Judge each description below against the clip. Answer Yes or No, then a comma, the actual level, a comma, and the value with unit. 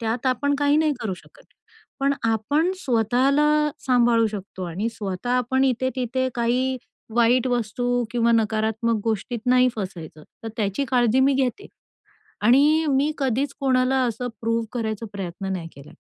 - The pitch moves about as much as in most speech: Yes, average, 3.0 semitones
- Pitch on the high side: Yes, high, 240 Hz